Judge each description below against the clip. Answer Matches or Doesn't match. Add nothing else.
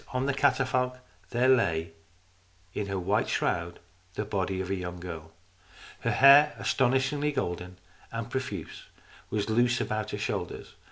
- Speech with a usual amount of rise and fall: Doesn't match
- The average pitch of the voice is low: Matches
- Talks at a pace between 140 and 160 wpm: Matches